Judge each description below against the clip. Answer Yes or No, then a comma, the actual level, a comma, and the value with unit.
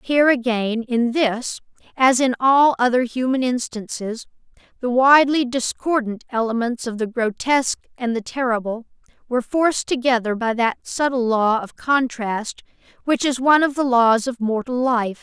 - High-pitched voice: Yes, high, 245 Hz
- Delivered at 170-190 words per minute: No, average, 150 wpm